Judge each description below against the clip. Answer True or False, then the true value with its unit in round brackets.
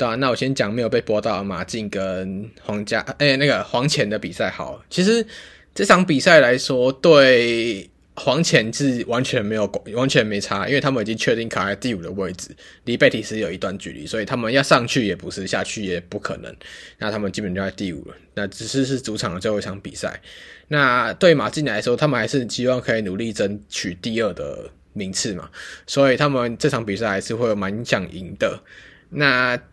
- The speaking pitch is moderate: False (115 Hz)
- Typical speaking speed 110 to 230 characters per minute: False (305 characters per minute)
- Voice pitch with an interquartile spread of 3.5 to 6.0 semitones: True (4.5 semitones)